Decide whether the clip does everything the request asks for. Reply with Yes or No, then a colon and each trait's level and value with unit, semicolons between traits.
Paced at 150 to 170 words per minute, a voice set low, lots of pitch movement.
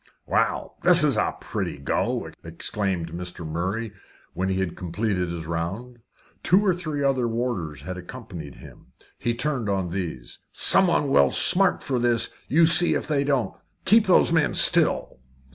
Yes: average, 160 wpm; low, 115 Hz; wide, 8.4 semitones